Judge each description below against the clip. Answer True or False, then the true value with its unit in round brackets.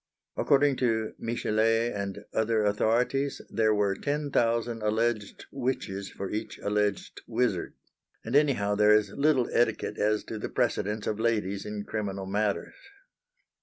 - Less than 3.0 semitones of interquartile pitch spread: True (2.4 semitones)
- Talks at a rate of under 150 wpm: True (135 wpm)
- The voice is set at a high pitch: False (110 Hz)